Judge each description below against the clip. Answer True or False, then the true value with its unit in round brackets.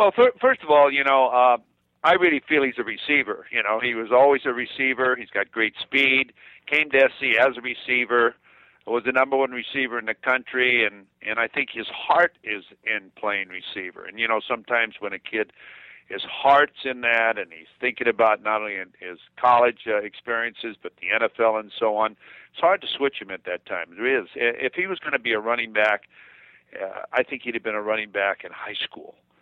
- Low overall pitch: True (120 Hz)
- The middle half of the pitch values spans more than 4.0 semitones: False (3.3 semitones)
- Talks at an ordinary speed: False (220 wpm)